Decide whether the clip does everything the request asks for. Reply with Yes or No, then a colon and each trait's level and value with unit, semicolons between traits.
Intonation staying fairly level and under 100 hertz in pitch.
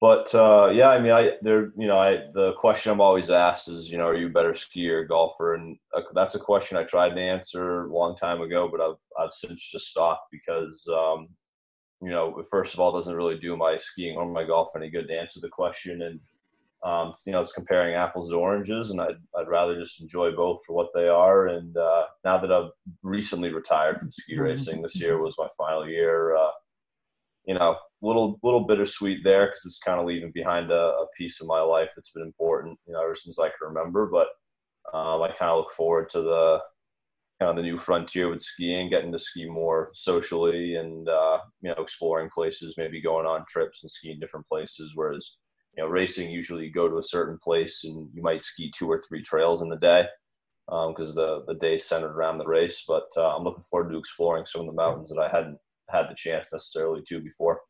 Yes: narrow, 2.2 semitones; very low, 85 Hz